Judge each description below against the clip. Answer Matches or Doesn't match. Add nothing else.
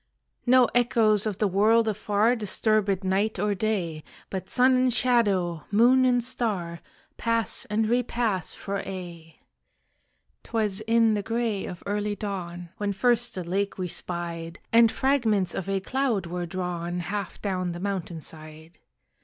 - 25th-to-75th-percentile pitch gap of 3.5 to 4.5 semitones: Matches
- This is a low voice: Doesn't match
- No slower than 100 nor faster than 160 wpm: Matches